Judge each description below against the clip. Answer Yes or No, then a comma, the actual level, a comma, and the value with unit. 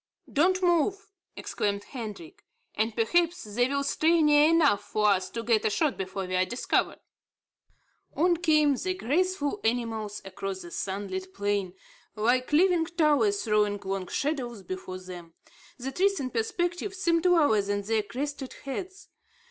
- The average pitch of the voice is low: No, high, 245 Hz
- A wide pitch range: Yes, wide, 8.5 semitones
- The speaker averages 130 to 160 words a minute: Yes, average, 150 wpm